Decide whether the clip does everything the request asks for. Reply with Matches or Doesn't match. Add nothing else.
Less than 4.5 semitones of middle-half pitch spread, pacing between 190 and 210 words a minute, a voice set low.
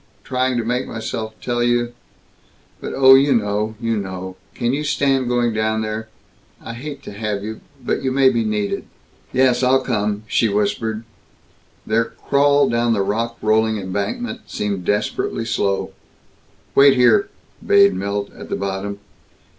Doesn't match